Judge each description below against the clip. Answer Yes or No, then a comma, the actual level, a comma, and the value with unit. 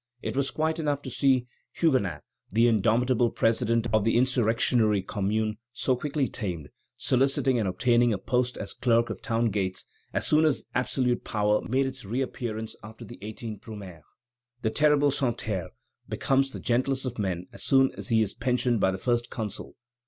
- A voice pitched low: Yes, low, 120 Hz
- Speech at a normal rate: Yes, average, 170 wpm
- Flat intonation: No, average, 3.5 semitones